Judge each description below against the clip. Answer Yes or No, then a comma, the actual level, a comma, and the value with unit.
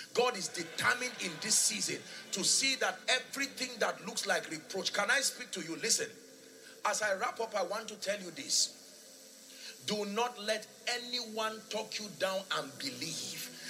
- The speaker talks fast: No, average, 170 wpm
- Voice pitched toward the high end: Yes, high, 225 Hz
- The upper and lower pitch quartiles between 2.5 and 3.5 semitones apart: Yes, average, 3.1 semitones